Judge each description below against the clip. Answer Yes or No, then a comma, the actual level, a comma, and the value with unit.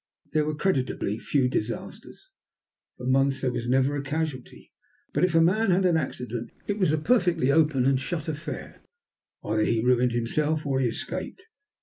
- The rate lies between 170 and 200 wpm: Yes, average, 175 wpm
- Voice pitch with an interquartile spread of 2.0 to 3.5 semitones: No, average, 4.4 semitones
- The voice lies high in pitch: No, medium, 140 Hz